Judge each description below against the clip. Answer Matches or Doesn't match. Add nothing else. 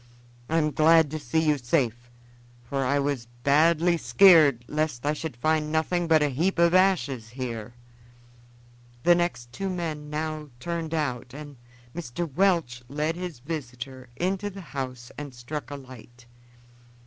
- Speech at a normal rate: Matches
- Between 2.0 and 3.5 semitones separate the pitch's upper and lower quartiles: Doesn't match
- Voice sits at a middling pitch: Matches